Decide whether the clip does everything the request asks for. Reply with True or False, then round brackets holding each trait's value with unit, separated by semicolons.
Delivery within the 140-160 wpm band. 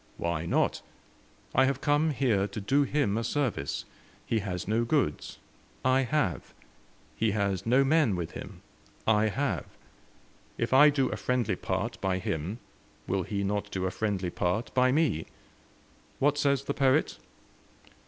True (155 wpm)